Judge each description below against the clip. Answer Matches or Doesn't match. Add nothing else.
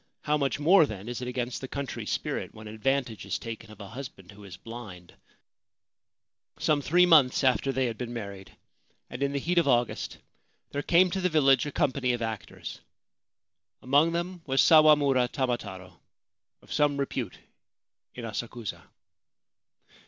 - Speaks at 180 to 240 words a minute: Doesn't match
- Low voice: Matches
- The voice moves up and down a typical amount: Matches